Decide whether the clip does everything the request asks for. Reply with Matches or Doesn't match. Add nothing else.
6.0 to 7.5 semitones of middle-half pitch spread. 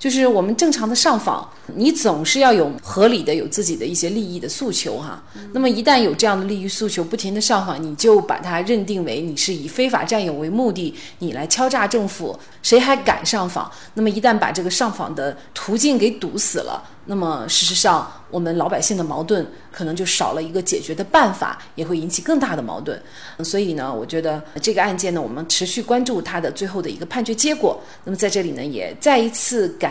Doesn't match